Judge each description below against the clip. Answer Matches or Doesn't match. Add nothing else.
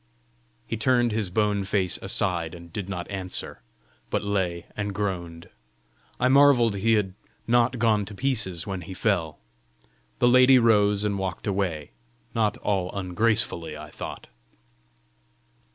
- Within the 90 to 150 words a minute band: Matches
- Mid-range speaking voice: Doesn't match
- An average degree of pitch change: Matches